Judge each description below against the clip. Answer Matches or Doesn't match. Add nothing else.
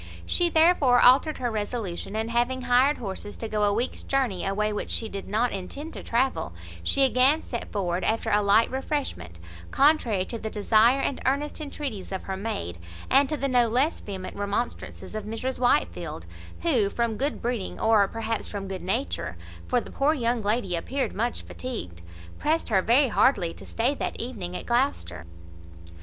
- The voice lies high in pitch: Matches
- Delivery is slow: Doesn't match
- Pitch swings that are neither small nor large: Matches